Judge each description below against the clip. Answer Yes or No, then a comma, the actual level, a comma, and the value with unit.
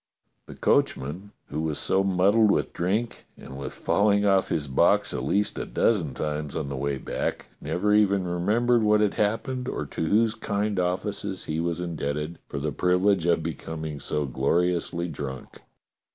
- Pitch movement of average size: Yes, average, 4.9 semitones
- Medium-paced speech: Yes, average, 165 wpm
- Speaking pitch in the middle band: No, very low, 90 Hz